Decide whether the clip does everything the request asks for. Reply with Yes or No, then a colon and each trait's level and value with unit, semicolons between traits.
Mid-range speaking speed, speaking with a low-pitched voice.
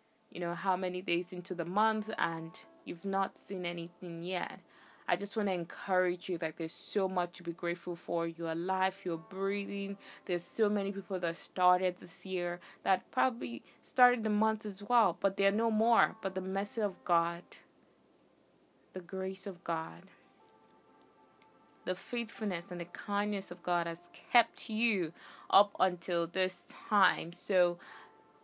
No: average, 160 wpm; medium, 185 Hz